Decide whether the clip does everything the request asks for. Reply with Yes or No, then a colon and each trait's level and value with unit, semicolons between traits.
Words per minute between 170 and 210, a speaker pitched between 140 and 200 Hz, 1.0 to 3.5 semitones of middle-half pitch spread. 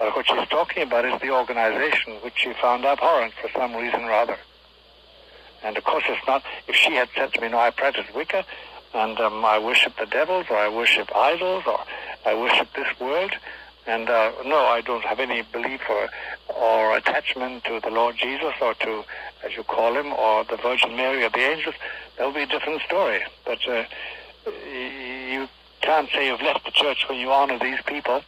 No: average, 200 wpm; low, 125 Hz; average, 3.2 semitones